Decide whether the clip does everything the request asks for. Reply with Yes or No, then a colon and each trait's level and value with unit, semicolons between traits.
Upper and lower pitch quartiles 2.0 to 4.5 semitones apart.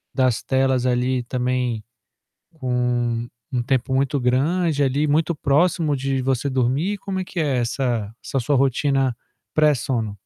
Yes: average, 2.8 semitones